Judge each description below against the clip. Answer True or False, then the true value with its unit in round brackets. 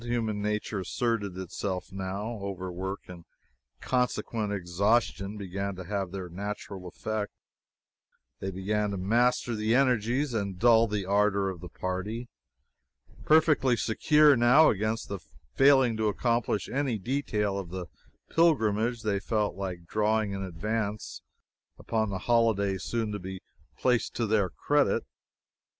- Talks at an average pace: False (130 wpm)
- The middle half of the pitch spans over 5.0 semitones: False (3.3 semitones)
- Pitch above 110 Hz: False (105 Hz)